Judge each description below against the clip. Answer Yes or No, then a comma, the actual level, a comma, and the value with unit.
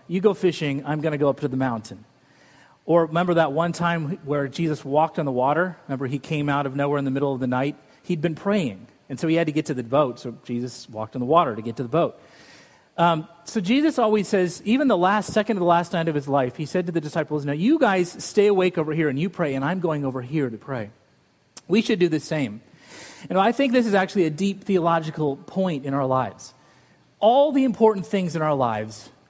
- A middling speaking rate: No, fast, 250 wpm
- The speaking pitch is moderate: Yes, medium, 160 Hz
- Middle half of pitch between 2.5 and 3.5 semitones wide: No, average, 4.9 semitones